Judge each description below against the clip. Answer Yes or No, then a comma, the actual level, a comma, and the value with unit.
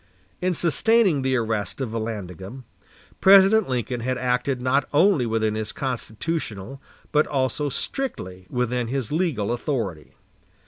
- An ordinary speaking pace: No, slow, 125 wpm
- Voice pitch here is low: Yes, low, 125 Hz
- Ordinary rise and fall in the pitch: Yes, average, 4.9 semitones